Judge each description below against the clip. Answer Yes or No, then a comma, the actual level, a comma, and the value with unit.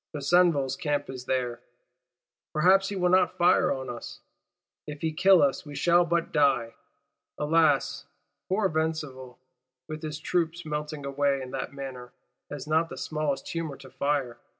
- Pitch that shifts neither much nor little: Yes, average, 3.5 semitones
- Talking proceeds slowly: No, average, 150 wpm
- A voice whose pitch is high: No, medium, 150 Hz